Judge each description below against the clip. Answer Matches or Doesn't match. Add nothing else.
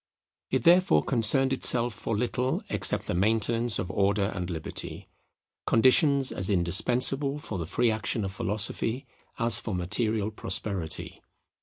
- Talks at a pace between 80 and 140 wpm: Matches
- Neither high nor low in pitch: Doesn't match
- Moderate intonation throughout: Matches